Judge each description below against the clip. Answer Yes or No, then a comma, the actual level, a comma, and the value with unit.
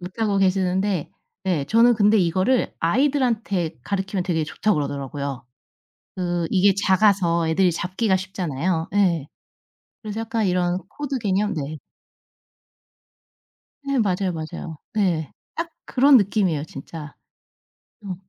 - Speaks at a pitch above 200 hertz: No, medium, 185 Hz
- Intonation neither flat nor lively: Yes, average, 4.1 semitones